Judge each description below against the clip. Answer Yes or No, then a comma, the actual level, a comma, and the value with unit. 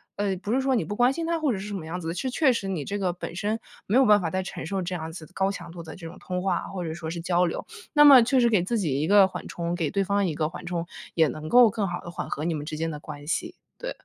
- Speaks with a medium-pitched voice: Yes, medium, 180 Hz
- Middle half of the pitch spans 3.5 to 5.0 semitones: Yes, average, 4.2 semitones